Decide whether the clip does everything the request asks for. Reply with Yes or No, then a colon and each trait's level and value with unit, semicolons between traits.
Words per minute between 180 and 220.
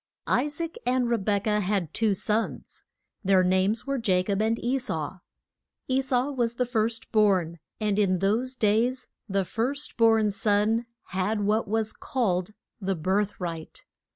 No: average, 160 wpm